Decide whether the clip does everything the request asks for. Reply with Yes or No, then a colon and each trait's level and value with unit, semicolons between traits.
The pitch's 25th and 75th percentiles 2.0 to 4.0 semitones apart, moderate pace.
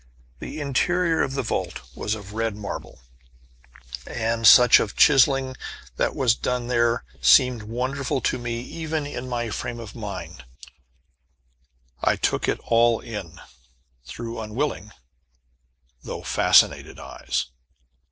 No: average, 3.1 semitones; slow, 125 wpm